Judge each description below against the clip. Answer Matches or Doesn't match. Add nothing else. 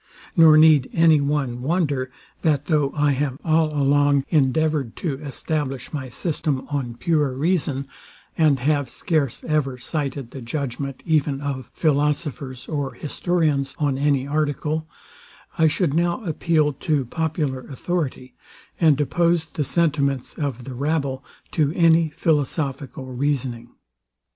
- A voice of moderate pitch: Matches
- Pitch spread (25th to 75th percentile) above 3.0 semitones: Doesn't match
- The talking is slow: Matches